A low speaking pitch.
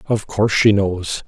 Yes: low, 100 Hz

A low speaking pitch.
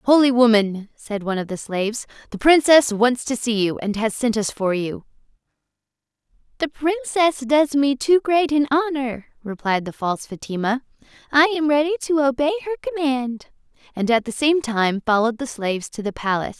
No: very high, 255 Hz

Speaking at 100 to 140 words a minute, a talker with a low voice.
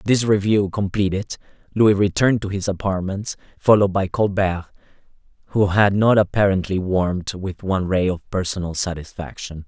Yes: slow, 135 wpm; very low, 95 Hz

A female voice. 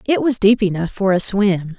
Yes: female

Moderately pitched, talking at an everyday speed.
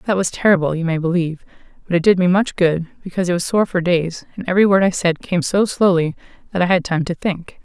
No: medium, 180 Hz; fast, 250 wpm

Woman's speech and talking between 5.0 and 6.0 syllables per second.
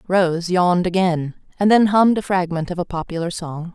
Yes: female; 5.3 syllables/s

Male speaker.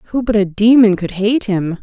No: female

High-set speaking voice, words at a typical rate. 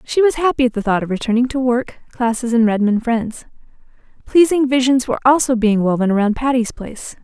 Yes: high, 240 Hz; average, 190 wpm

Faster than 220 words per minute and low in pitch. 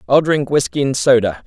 No: fast, 205 wpm; low, 130 Hz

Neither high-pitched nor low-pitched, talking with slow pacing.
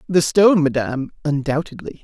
Yes: medium, 150 Hz; slow, 120 wpm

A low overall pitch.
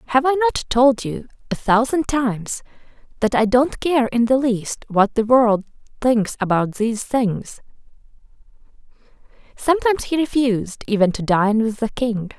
No: high, 240 Hz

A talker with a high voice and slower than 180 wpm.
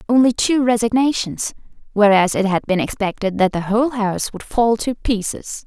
Yes: high, 220 Hz; average, 160 wpm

